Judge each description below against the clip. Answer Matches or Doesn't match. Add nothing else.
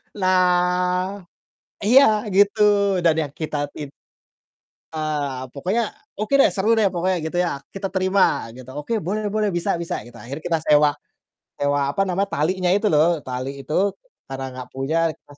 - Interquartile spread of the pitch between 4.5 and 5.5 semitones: Matches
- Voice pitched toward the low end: Doesn't match